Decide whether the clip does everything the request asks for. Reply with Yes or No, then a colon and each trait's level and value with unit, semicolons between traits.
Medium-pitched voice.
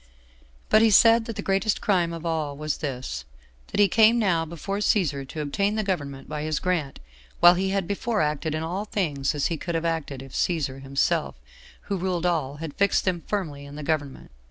Yes: medium, 165 Hz